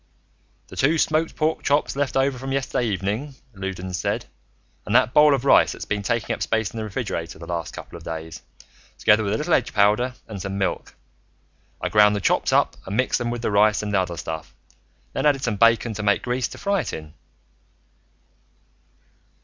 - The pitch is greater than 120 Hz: No, low, 110 Hz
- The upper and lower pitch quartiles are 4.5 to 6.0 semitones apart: Yes, wide, 5.4 semitones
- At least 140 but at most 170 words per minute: No, average, 200 wpm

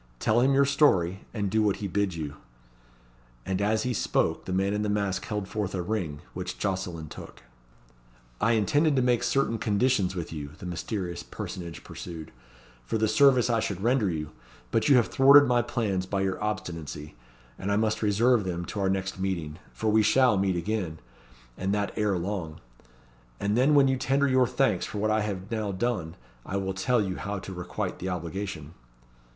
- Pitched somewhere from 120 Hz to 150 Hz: No, low, 100 Hz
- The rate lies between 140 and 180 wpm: No, average, 190 wpm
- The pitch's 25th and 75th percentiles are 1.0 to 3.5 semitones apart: No, average, 3.9 semitones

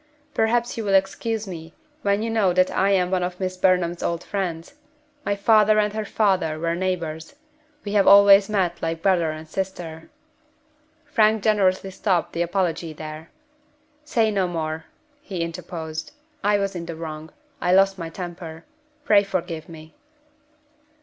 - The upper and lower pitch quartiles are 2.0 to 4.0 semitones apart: Yes, average, 3.4 semitones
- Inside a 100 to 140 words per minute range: No, average, 160 wpm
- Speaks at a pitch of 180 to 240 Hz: Yes, medium, 185 Hz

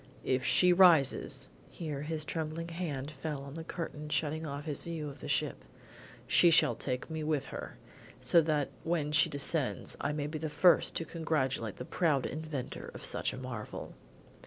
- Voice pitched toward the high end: No, medium, 150 Hz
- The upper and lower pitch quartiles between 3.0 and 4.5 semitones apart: No, narrow, 2.6 semitones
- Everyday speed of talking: Yes, average, 185 wpm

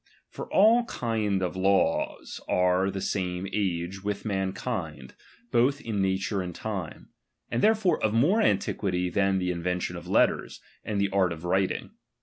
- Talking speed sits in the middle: Yes, average, 175 wpm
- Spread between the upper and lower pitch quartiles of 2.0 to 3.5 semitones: Yes, average, 3.1 semitones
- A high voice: No, very low, 95 Hz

